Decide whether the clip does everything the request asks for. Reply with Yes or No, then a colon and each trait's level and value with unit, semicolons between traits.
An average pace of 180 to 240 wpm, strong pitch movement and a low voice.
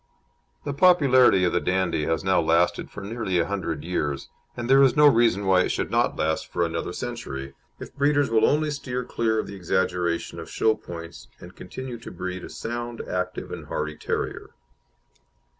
Yes: average, 185 wpm; wide, 6.0 semitones; very low, 95 Hz